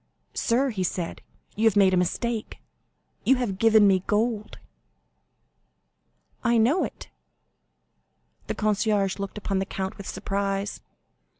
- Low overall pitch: No, high, 205 Hz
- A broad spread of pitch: No, average, 2.7 semitones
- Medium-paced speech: No, slow, 125 wpm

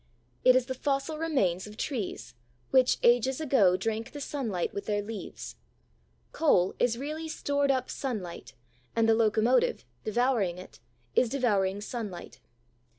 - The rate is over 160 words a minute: No, average, 140 wpm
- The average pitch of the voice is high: Yes, high, 230 Hz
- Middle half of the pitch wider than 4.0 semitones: Yes, average, 4.9 semitones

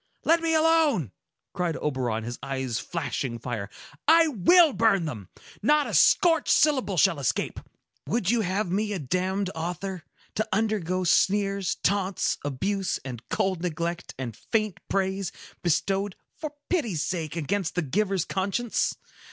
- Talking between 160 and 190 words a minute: No, slow, 135 wpm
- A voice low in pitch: No, high, 190 Hz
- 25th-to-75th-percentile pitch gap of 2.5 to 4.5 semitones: No, average, 5.2 semitones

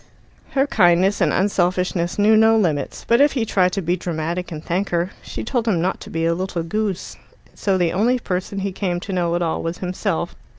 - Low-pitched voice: No, medium, 185 Hz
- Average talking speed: No, fast, 220 wpm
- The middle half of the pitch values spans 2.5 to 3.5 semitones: Yes, average, 3.1 semitones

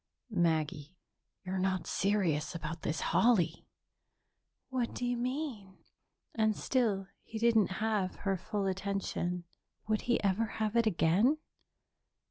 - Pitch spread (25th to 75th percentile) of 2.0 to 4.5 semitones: Yes, average, 4.0 semitones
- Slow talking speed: Yes, slow, 120 wpm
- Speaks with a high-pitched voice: Yes, high, 200 Hz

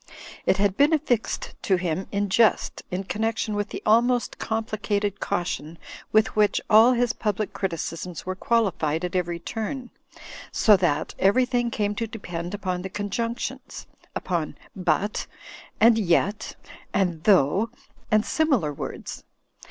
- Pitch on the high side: Yes, high, 205 Hz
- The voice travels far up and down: No, average, 3.7 semitones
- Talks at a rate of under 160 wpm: Yes, slow, 135 wpm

